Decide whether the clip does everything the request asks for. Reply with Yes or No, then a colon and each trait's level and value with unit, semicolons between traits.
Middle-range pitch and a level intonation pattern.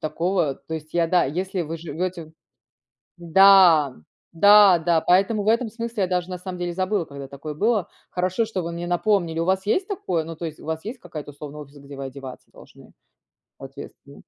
No: medium, 175 Hz; average, 3.7 semitones